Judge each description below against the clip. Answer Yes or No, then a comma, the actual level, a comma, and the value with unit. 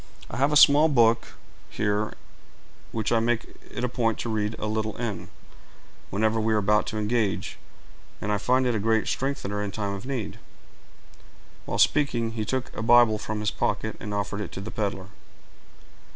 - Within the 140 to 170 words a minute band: No, average, 180 wpm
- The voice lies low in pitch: Yes, low, 110 Hz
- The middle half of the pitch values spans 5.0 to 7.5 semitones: No, narrow, 2.4 semitones